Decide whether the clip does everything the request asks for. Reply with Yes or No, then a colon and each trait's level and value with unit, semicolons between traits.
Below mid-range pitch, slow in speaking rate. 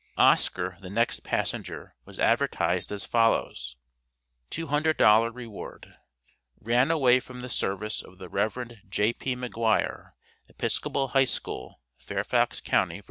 Yes: low, 115 Hz; slow, 120 wpm